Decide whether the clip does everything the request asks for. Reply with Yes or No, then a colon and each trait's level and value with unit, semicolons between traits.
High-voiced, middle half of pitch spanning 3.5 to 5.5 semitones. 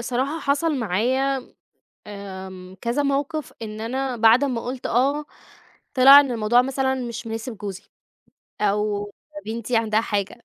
Yes: high, 240 Hz; average, 4.0 semitones